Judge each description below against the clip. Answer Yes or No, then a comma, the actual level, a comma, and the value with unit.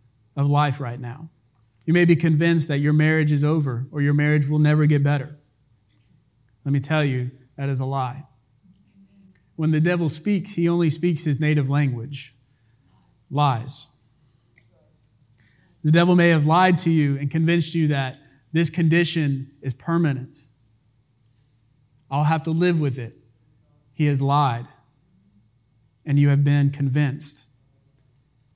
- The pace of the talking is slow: No, average, 145 wpm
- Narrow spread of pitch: No, average, 3.5 semitones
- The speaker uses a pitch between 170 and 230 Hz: No, medium, 140 Hz